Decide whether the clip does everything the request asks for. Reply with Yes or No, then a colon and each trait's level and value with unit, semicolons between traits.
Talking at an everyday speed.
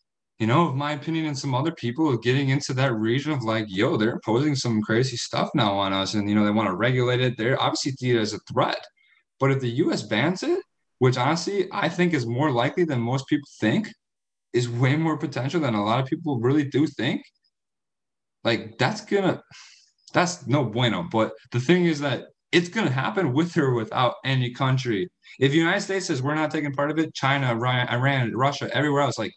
No: fast, 215 wpm